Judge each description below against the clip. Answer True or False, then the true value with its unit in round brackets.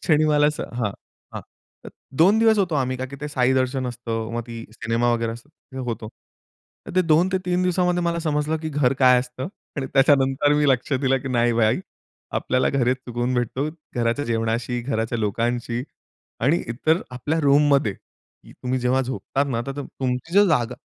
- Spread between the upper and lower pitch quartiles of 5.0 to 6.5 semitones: False (3.7 semitones)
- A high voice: False (130 Hz)